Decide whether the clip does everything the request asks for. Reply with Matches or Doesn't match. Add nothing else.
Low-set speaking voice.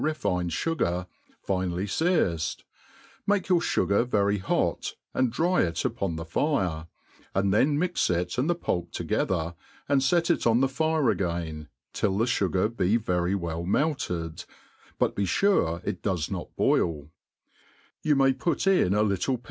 Matches